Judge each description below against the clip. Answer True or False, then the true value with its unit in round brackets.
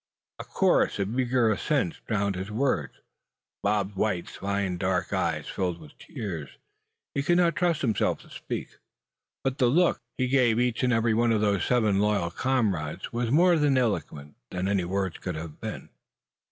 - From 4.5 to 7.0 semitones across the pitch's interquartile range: True (5.1 semitones)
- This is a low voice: True (105 Hz)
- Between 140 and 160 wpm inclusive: False (170 wpm)